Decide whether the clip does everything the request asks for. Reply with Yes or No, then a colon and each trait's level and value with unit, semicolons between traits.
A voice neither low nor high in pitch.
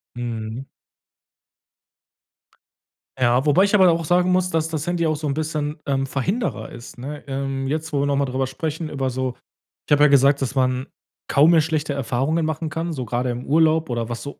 Yes: medium, 145 Hz